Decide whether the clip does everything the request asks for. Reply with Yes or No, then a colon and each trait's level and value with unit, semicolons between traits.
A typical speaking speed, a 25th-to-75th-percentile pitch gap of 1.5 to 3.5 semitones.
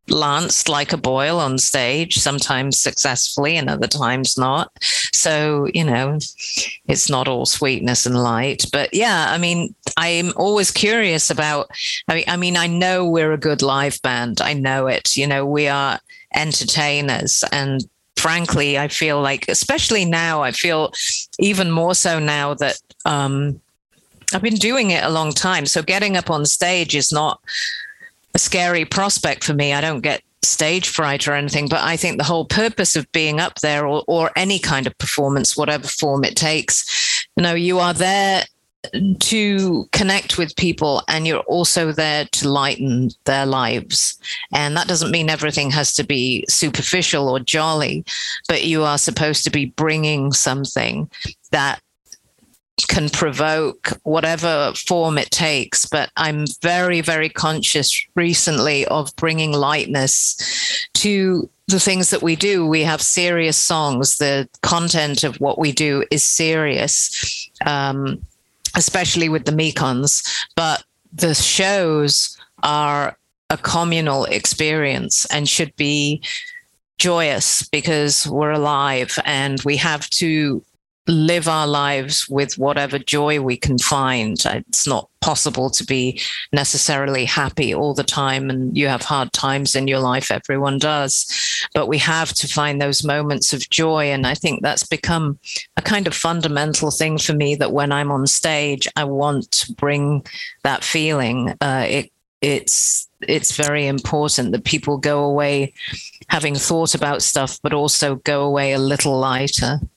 Yes: average, 155 wpm; average, 3.0 semitones